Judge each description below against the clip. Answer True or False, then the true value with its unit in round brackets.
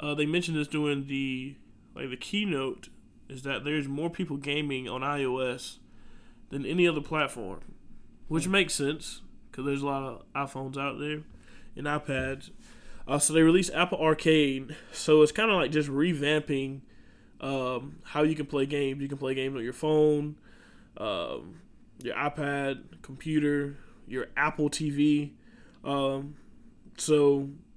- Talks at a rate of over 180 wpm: False (150 wpm)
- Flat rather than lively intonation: True (2.1 semitones)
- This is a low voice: False (145 Hz)